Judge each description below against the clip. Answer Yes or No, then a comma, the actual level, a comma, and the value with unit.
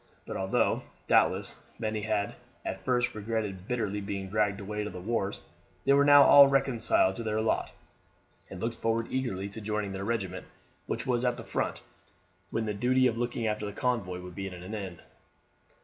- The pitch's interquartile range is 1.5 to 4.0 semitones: Yes, average, 3.3 semitones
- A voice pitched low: Yes, low, 110 Hz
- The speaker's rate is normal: Yes, average, 185 wpm